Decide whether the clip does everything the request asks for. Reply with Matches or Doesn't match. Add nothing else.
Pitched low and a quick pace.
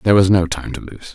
Matches